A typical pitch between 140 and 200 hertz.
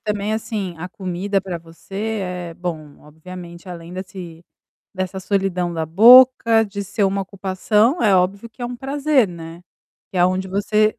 Yes: high, 190 Hz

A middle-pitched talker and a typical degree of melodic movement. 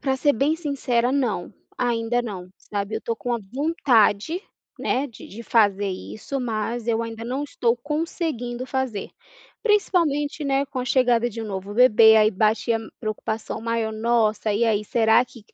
No: high, 235 Hz; average, 3.4 semitones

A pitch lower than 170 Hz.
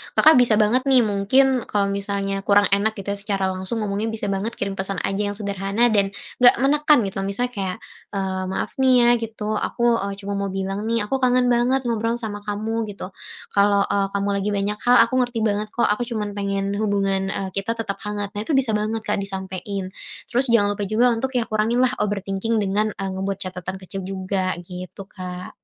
No: high, 205 Hz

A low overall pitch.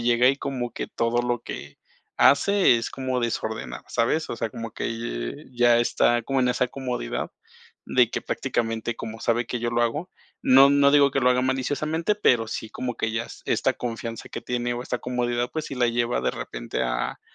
Yes: low, 120 Hz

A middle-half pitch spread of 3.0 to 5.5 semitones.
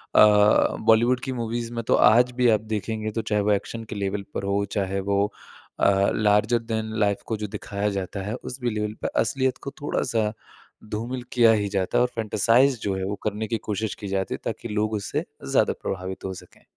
No: narrow, 2.4 semitones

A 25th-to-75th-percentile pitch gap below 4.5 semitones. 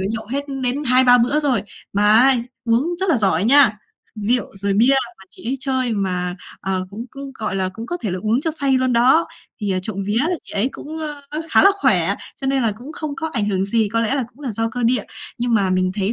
No: average, 4.8 semitones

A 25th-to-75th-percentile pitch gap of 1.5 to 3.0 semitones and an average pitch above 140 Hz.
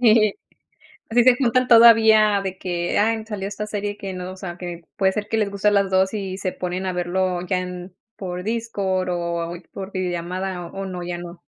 Yes: average, 2.7 semitones; high, 190 Hz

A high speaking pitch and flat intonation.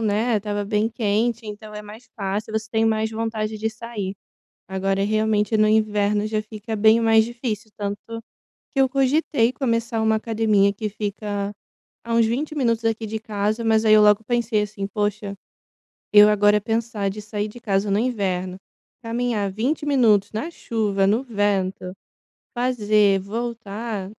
Yes: high, 215 Hz; narrow, 1.9 semitones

